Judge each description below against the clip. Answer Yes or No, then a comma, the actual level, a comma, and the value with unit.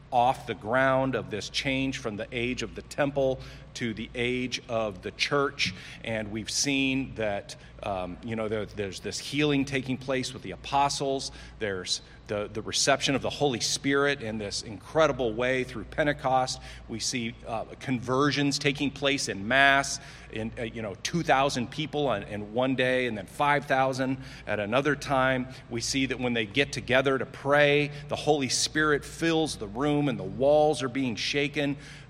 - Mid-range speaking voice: No, low, 130 Hz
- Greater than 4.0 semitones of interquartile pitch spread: No, average, 3.5 semitones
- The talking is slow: No, average, 180 wpm